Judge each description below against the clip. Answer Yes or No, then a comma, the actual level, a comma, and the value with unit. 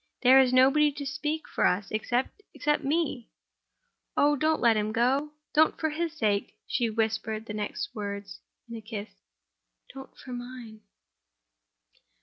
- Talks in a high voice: Yes, very high, 250 Hz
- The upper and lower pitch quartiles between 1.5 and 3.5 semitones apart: No, average, 5.3 semitones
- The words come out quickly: No, slow, 135 wpm